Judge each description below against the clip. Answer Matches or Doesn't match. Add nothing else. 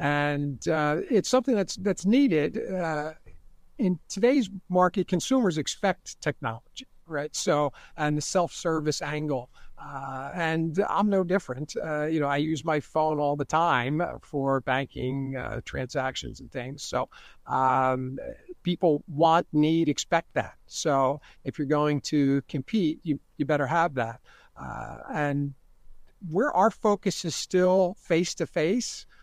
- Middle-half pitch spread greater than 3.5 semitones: Matches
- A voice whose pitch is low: Doesn't match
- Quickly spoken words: Doesn't match